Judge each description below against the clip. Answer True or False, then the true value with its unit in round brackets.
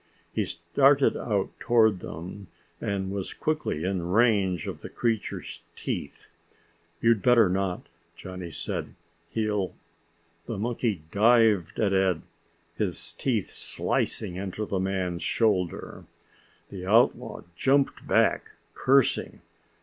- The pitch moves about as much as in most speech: True (3.8 semitones)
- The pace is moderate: False (115 wpm)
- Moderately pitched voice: False (100 Hz)